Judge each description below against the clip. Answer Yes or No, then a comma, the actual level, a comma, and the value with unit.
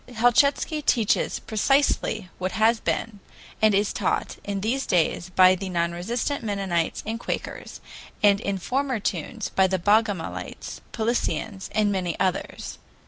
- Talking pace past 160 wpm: No, average, 140 wpm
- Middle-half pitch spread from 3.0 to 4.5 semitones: Yes, average, 3.6 semitones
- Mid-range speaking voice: No, high, 205 Hz